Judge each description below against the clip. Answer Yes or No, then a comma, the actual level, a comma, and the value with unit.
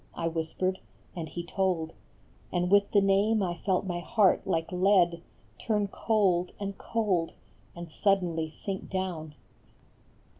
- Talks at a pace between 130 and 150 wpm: Yes, slow, 135 wpm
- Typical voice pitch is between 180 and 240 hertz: Yes, medium, 185 Hz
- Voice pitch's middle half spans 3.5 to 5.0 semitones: No, narrow, 2.5 semitones